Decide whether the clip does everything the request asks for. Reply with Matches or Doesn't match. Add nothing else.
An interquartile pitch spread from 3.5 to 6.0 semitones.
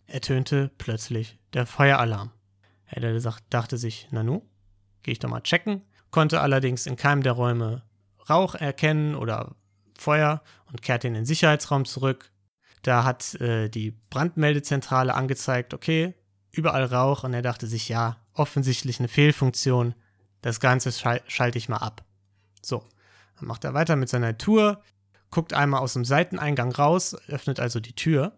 Matches